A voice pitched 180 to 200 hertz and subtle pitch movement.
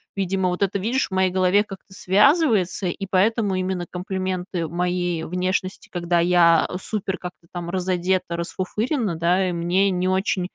Yes: medium, 185 Hz; narrow, 1.5 semitones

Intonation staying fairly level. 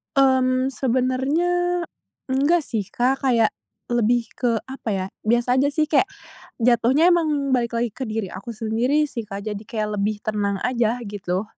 No: average, 4.0 semitones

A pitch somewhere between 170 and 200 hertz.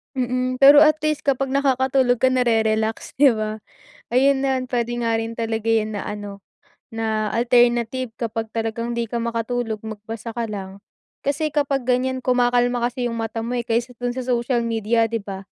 No: high, 240 Hz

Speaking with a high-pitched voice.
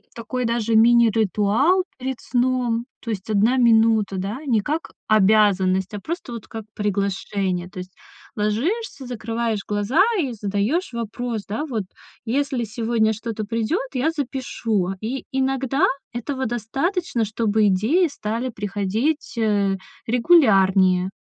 Yes: high, 225 Hz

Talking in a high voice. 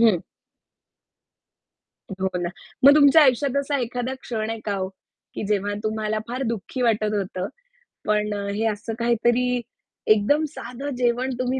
Yes: high, 230 Hz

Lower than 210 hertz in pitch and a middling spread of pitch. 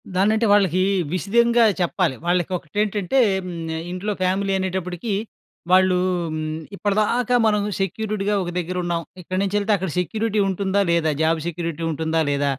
Yes: medium, 185 Hz; average, 3.3 semitones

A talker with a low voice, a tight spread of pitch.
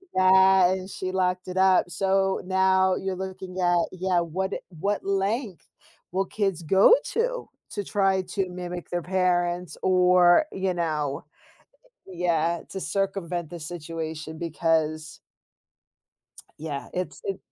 No: medium, 185 Hz; narrow, 1.8 semitones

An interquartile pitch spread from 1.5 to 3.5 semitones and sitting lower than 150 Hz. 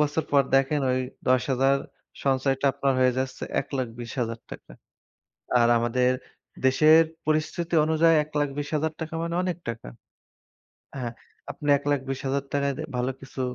Yes: average, 2.8 semitones; low, 135 Hz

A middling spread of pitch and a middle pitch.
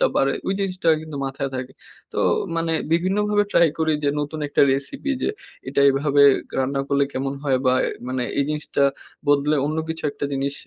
Yes: average, 3.2 semitones; medium, 145 Hz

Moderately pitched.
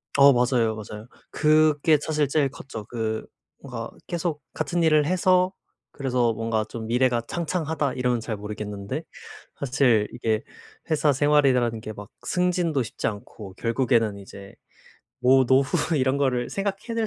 No: low, 130 Hz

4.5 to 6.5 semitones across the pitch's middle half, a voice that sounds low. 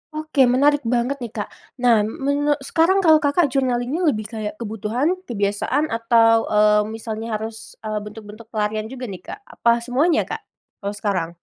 No: average, 4.9 semitones; high, 230 Hz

